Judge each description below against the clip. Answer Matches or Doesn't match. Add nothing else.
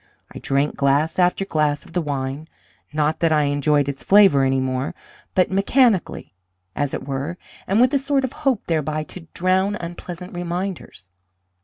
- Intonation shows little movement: Doesn't match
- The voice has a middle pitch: Matches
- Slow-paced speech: Doesn't match